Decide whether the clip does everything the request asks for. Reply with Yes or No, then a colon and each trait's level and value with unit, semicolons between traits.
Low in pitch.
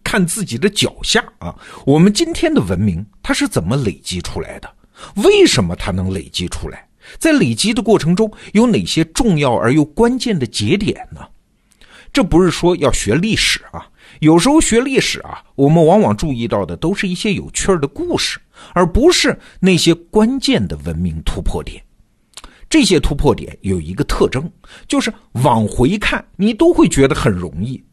No: medium, 175 Hz